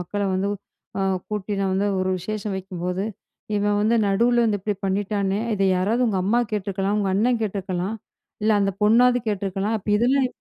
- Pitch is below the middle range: No, high, 205 Hz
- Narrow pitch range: Yes, narrow, 2.0 semitones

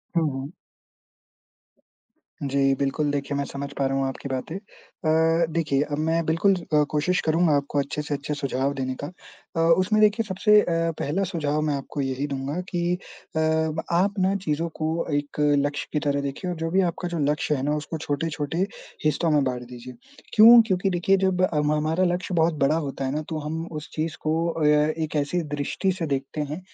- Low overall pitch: No, medium, 155 Hz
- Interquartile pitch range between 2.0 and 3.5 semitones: Yes, average, 3.1 semitones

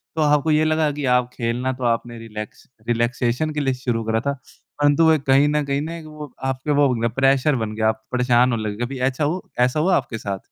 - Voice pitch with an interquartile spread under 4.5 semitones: Yes, average, 3.9 semitones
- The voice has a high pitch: No, low, 130 Hz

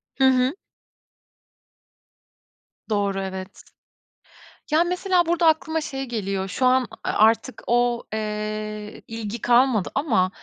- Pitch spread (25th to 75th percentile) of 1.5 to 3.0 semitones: No, average, 4.3 semitones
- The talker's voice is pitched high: Yes, high, 235 Hz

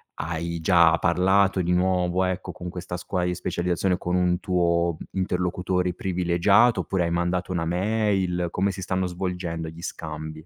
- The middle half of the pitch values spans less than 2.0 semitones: Yes, narrow, 1.3 semitones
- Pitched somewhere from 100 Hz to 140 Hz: No, very low, 90 Hz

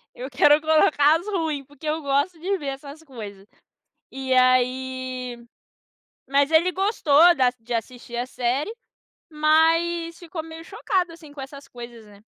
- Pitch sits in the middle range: No, very high, 285 Hz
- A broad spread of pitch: No, average, 4.2 semitones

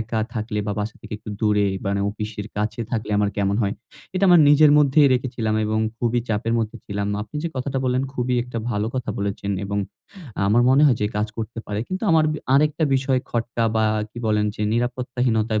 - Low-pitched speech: Yes, low, 115 Hz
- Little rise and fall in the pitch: No, average, 3.3 semitones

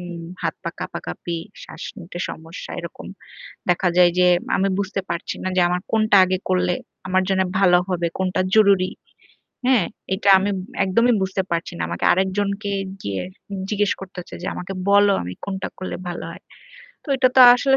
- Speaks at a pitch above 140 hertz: Yes, medium, 185 Hz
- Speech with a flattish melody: Yes, narrow, 2.2 semitones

